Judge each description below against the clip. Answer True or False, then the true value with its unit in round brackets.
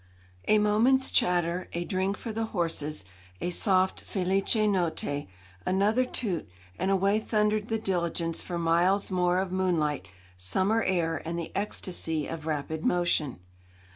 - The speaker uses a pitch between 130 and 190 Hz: True (185 Hz)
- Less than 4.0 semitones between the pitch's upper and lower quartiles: True (3.6 semitones)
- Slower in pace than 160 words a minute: True (140 wpm)